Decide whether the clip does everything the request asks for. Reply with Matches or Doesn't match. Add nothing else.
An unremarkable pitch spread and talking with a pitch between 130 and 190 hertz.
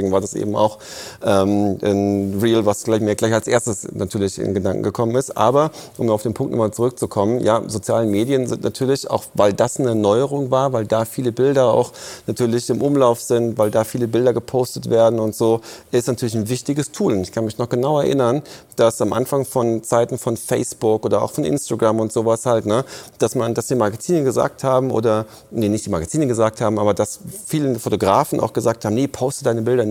Doesn't match